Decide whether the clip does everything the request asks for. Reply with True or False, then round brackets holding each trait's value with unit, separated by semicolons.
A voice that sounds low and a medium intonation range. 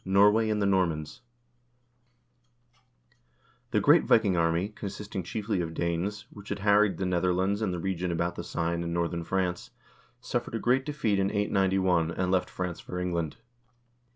True (95 Hz; 3.0 semitones)